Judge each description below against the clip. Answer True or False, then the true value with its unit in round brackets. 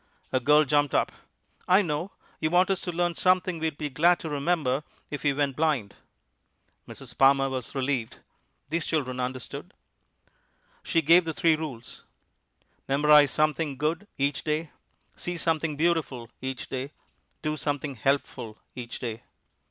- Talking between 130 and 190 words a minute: True (145 wpm)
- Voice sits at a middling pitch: True (150 Hz)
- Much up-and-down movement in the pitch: False (3.5 semitones)